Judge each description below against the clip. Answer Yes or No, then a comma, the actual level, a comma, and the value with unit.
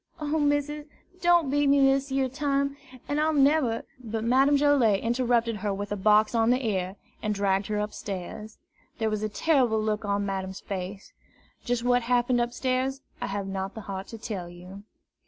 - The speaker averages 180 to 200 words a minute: Yes, average, 185 wpm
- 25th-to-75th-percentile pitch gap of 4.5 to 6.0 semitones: Yes, average, 5.0 semitones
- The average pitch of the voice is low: No, high, 230 Hz